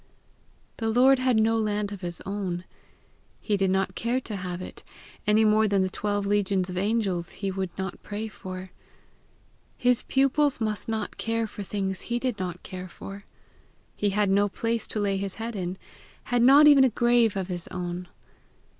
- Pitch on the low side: No, high, 205 Hz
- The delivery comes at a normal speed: Yes, average, 180 wpm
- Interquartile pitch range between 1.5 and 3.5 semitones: Yes, average, 3.2 semitones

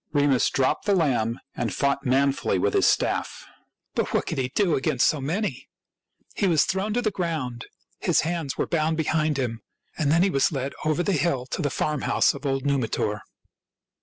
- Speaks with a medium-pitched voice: Yes, medium, 145 Hz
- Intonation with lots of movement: No, average, 4.1 semitones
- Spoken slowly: No, average, 190 wpm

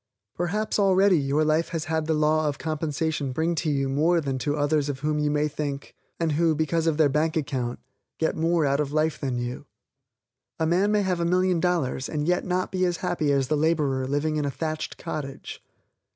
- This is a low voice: No, medium, 155 Hz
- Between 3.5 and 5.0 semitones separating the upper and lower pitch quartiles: No, average, 2.7 semitones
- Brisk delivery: Yes, fast, 210 wpm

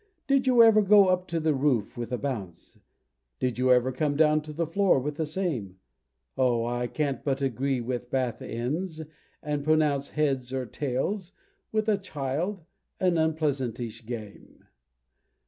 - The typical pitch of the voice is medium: Yes, medium, 145 Hz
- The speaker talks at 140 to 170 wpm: Yes, average, 160 wpm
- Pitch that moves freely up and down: No, average, 4.8 semitones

